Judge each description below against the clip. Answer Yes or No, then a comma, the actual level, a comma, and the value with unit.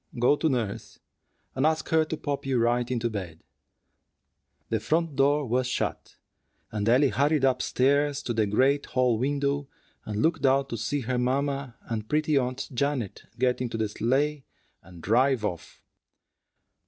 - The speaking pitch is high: No, low, 130 Hz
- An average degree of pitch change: Yes, average, 3.4 semitones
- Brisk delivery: No, average, 160 wpm